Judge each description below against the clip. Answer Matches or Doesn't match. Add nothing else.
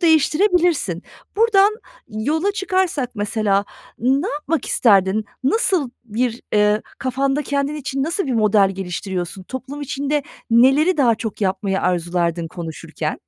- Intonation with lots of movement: Matches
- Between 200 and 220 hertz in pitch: Doesn't match